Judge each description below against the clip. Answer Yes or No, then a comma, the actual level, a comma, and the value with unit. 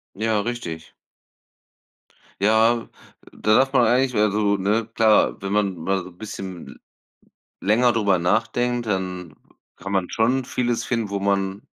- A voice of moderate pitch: No, low, 105 Hz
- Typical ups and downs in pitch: Yes, average, 3.1 semitones